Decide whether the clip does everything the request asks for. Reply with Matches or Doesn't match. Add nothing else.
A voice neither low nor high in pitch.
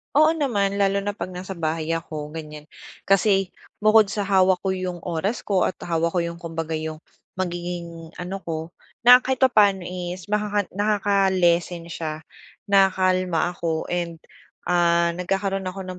Matches